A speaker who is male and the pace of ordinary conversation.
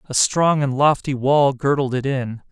Yes: male; average, 190 wpm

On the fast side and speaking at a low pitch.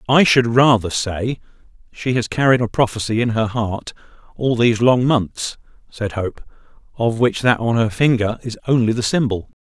No: average, 175 wpm; low, 115 Hz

